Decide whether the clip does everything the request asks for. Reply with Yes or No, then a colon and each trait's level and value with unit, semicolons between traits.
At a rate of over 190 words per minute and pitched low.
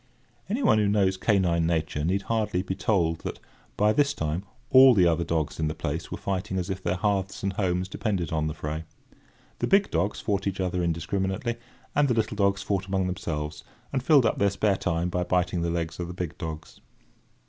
Yes: fast, 205 wpm; very low, 95 Hz